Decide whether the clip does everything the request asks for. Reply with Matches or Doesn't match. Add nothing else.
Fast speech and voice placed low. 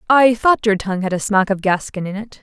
Doesn't match